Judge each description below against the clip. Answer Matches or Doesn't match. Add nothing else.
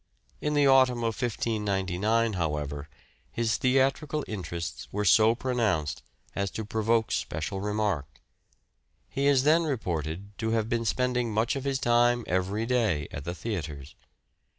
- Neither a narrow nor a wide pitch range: Matches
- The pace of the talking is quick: Doesn't match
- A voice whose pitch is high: Doesn't match